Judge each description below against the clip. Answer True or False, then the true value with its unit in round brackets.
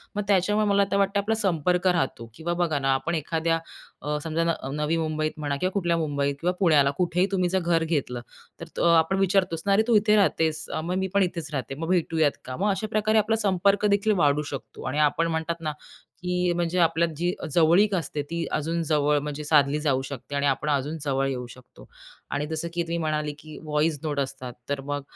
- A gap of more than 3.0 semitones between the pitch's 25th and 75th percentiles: True (3.7 semitones)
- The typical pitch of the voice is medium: True (165 Hz)